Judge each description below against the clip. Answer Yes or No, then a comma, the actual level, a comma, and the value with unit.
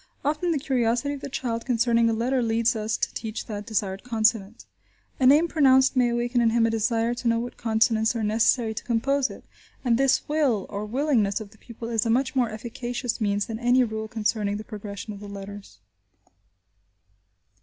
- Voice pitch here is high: Yes, high, 230 Hz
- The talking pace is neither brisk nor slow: Yes, average, 195 wpm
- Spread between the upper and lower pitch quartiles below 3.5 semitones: Yes, narrow, 2.4 semitones